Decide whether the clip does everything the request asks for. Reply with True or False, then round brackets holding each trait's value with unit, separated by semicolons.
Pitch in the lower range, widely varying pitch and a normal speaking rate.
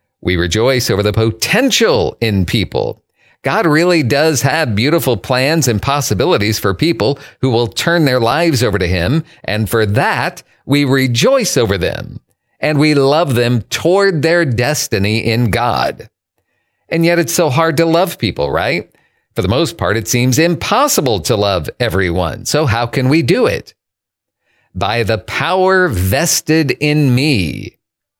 True (130 Hz; 6.3 semitones; 155 wpm)